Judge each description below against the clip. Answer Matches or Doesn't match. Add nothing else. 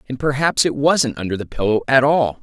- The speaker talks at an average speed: Doesn't match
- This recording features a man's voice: Matches